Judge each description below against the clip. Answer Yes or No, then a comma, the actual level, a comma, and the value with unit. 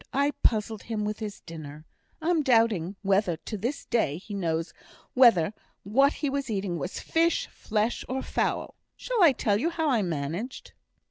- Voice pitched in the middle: No, high, 215 Hz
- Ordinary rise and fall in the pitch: No, wide, 6.6 semitones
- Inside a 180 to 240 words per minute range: No, average, 165 wpm